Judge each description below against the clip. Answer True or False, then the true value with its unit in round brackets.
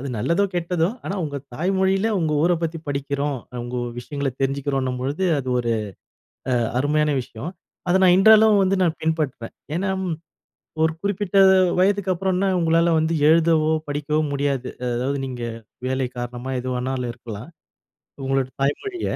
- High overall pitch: False (150 Hz)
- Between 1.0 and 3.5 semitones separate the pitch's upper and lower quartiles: False (5.2 semitones)